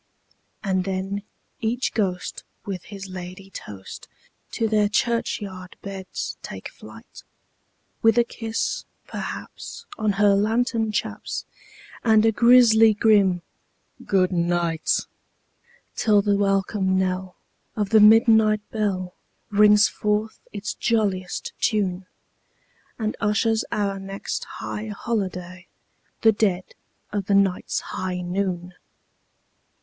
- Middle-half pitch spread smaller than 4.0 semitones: Yes, narrow, 2.6 semitones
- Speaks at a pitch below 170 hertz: No, high, 200 Hz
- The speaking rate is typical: No, slow, 105 wpm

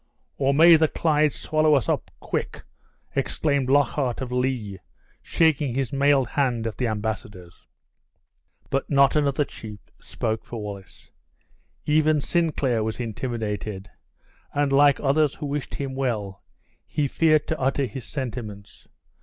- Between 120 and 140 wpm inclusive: Yes, slow, 135 wpm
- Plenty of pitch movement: No, average, 4.6 semitones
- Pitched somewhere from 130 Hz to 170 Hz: Yes, low, 135 Hz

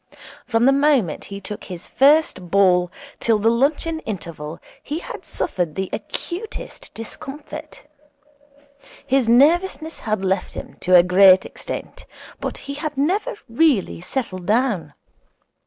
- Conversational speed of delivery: No, slow, 130 wpm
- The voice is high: Yes, high, 230 Hz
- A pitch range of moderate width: No, wide, 8.1 semitones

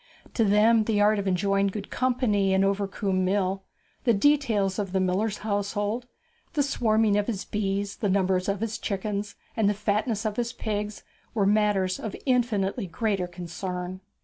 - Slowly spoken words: No, average, 165 wpm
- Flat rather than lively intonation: Yes, narrow, 2.0 semitones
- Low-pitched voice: No, high, 205 Hz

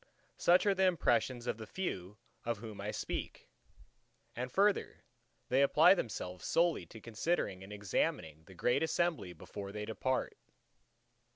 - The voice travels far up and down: Yes, wide, 8.7 semitones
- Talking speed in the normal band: Yes, average, 145 wpm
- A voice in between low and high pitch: No, low, 115 Hz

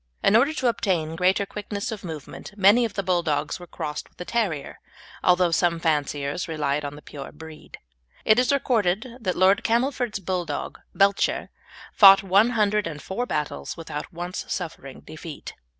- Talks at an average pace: Yes, average, 165 wpm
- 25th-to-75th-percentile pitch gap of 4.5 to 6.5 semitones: Yes, average, 5.0 semitones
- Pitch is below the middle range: No, medium, 185 Hz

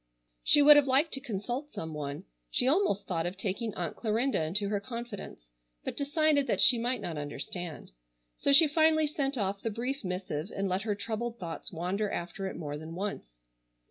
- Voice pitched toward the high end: Yes, high, 210 Hz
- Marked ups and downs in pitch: Yes, wide, 7.3 semitones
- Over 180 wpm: Yes, average, 190 wpm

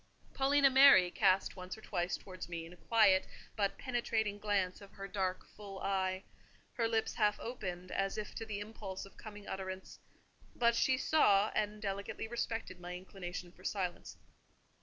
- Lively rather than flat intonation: No, average, 3.0 semitones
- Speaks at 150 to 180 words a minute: Yes, average, 160 wpm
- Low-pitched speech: No, high, 200 Hz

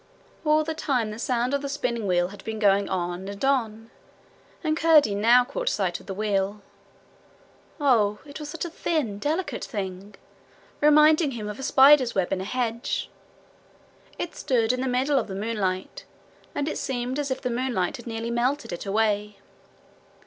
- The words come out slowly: No, average, 175 wpm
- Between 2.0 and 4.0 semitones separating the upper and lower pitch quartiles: No, wide, 5.4 semitones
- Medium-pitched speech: No, high, 235 Hz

